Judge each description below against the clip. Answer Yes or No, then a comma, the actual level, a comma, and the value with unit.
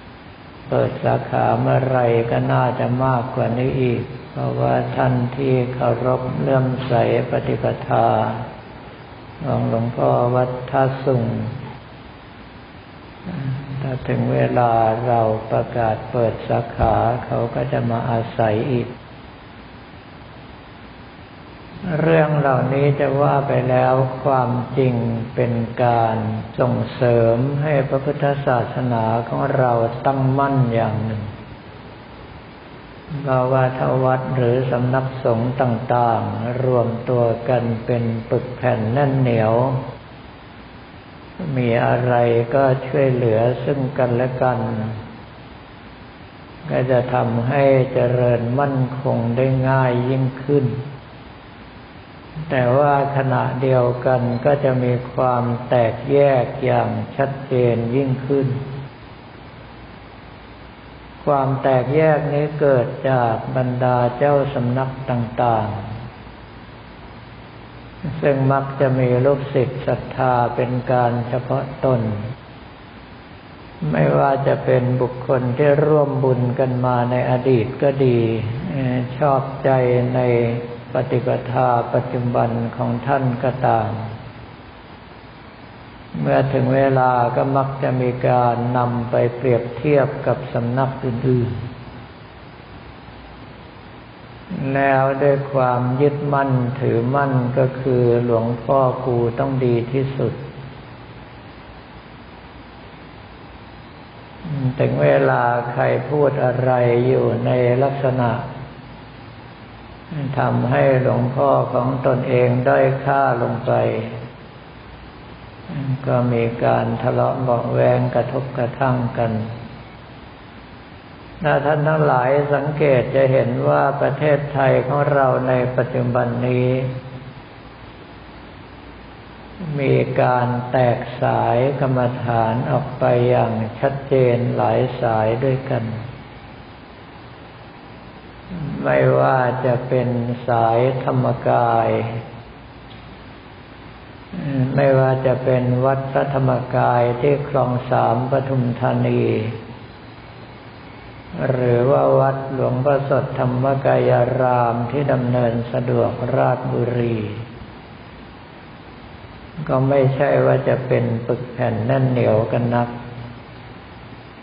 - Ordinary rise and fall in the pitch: No, narrow, 2.0 semitones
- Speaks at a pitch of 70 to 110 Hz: No, low, 125 Hz